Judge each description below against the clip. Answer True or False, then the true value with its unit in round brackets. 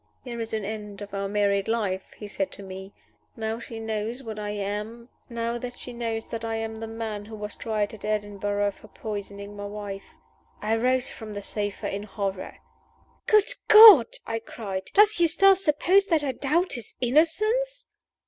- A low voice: False (220 Hz)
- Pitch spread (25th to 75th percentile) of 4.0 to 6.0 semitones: False (3.4 semitones)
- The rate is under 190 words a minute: True (160 wpm)